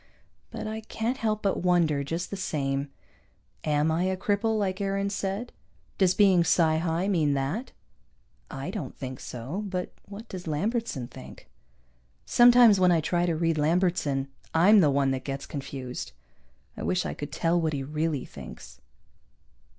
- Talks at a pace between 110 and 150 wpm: No, average, 160 wpm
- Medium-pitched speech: Yes, medium, 175 Hz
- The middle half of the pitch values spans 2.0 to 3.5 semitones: No, average, 5.3 semitones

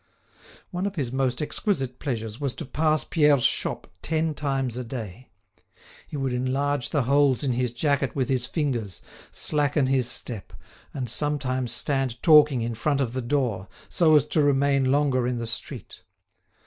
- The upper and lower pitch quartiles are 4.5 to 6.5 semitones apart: No, average, 2.9 semitones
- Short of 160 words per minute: No, average, 165 wpm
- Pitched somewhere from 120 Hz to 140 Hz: Yes, low, 135 Hz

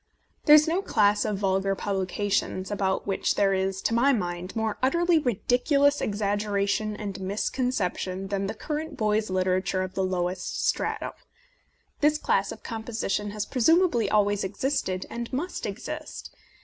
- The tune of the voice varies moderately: Yes, average, 4.2 semitones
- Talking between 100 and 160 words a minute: Yes, average, 150 wpm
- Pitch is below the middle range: No, high, 205 Hz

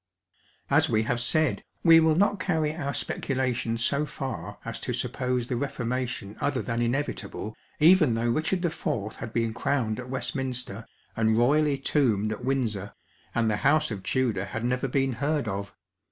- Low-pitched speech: Yes, low, 125 Hz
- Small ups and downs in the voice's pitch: No, average, 4.0 semitones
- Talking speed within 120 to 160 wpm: No, average, 170 wpm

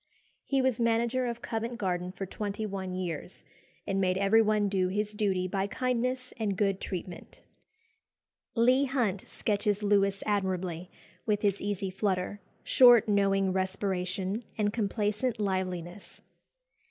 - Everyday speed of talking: No, slow, 130 wpm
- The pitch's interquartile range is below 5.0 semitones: Yes, average, 2.9 semitones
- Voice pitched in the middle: No, high, 200 Hz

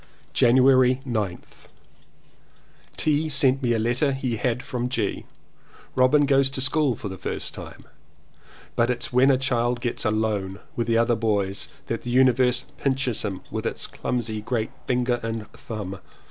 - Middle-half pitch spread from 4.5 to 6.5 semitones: No, average, 2.7 semitones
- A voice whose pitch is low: Yes, low, 120 Hz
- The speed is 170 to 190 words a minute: No, average, 155 wpm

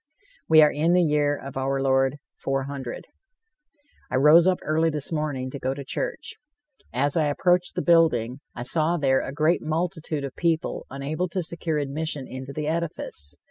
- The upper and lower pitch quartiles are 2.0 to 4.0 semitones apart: Yes, average, 3.3 semitones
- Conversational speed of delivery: Yes, average, 175 wpm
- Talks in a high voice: No, medium, 150 Hz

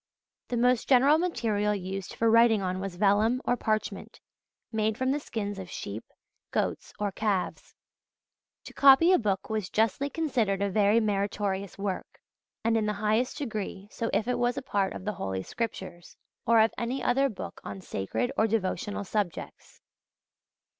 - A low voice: No, high, 215 Hz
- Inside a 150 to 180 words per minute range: Yes, average, 165 wpm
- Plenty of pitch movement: No, average, 3.5 semitones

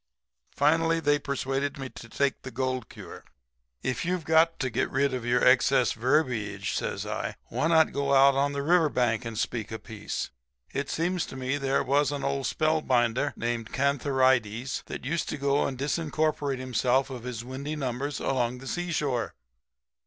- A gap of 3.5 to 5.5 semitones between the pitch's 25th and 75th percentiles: No, average, 2.8 semitones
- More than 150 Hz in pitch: No, low, 135 Hz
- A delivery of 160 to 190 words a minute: Yes, average, 175 wpm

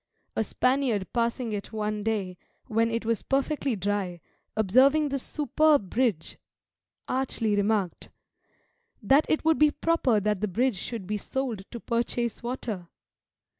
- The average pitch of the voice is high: Yes, high, 230 Hz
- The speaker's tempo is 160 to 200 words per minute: No, slow, 135 wpm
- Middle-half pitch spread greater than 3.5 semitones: Yes, average, 4.4 semitones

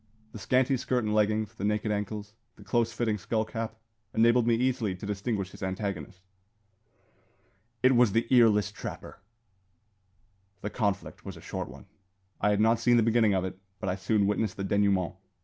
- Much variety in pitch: No, narrow, 2.4 semitones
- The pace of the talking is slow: No, average, 175 wpm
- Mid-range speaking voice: No, low, 105 Hz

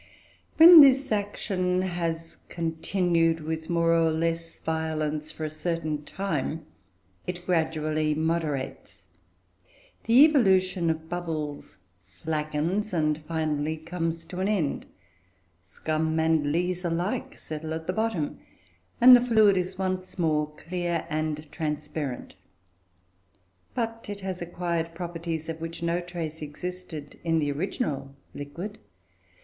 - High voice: No, medium, 165 Hz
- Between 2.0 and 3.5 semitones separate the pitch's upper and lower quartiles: Yes, narrow, 2.6 semitones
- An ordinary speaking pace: No, slow, 120 wpm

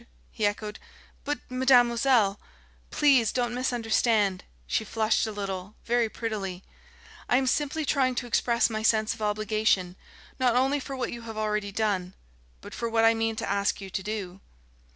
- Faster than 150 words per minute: Yes, average, 170 wpm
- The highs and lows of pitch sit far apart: No, average, 2.8 semitones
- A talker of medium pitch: No, high, 225 Hz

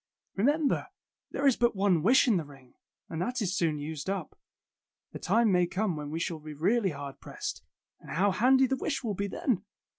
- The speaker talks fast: Yes, fast, 210 wpm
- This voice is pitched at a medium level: No, high, 195 Hz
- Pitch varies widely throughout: Yes, wide, 6.8 semitones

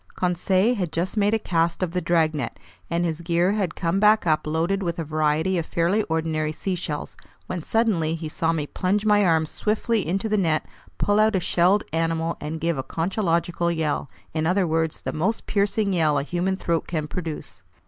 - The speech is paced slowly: No, average, 195 wpm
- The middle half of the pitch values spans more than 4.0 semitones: No, average, 3.2 semitones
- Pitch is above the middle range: No, medium, 170 Hz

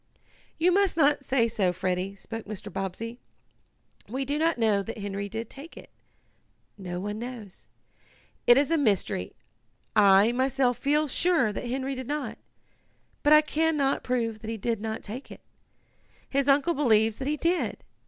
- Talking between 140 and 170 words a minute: Yes, average, 165 wpm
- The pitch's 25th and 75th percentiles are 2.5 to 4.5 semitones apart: No, average, 5.3 semitones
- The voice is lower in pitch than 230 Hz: No, high, 240 Hz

